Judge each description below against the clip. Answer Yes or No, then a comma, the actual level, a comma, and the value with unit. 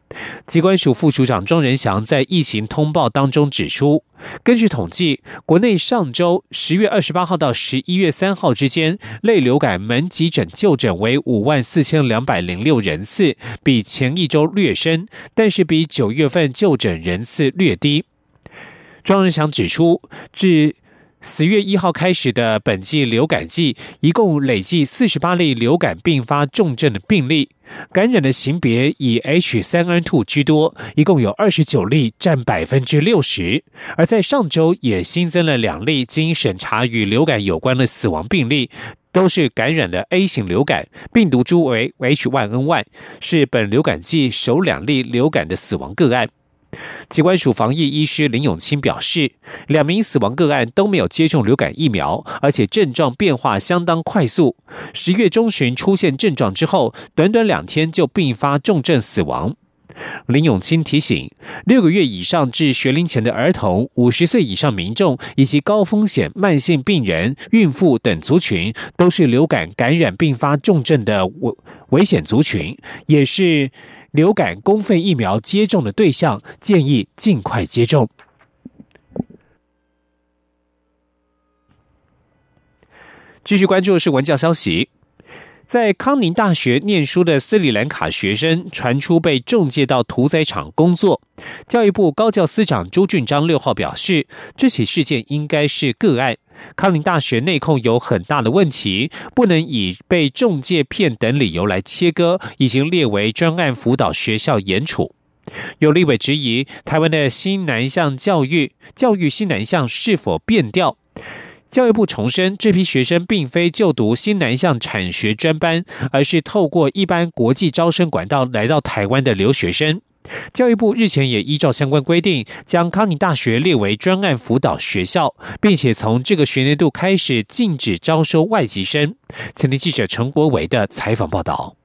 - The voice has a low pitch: No, medium, 150 Hz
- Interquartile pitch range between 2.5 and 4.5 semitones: No, wide, 5.5 semitones